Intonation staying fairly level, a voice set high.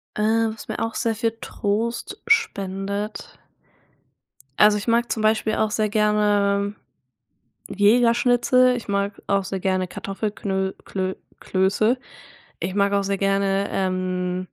Yes: narrow, 2.3 semitones; high, 205 Hz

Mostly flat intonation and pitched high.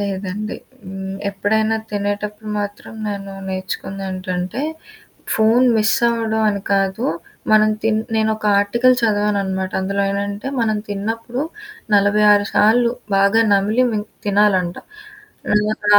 Yes: narrow, 1.8 semitones; high, 205 Hz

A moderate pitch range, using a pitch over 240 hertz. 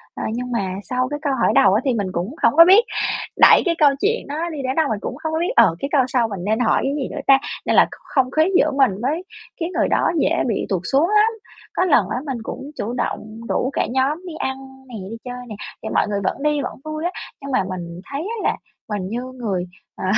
No: wide, 5.8 semitones; very high, 260 Hz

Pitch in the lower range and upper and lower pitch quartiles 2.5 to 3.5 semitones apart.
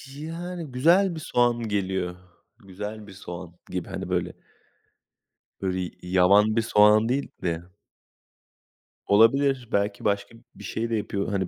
No: low, 105 Hz; average, 4.7 semitones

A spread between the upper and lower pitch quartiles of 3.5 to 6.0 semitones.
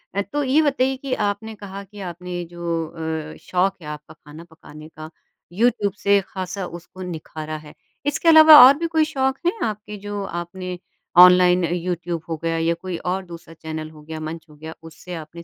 Yes: average, 4.3 semitones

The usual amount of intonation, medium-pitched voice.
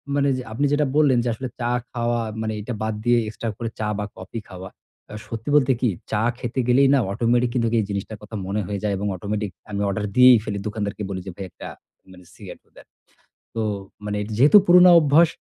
No: average, 3.5 semitones; low, 115 Hz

